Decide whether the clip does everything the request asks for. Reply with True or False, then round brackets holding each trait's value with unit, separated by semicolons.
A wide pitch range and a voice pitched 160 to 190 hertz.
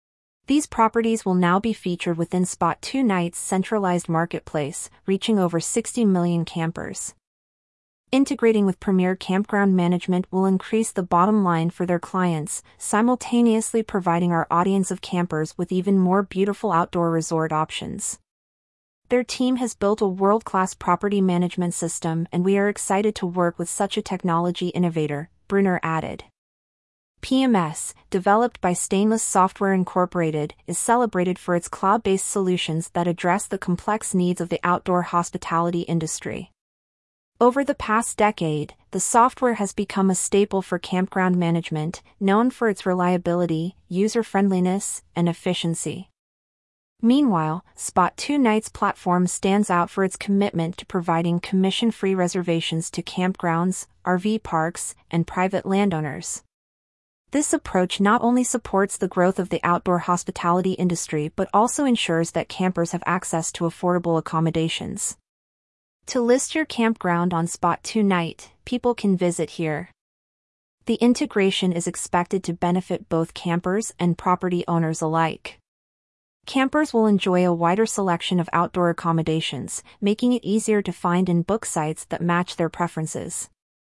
False (3.1 semitones; 185 Hz)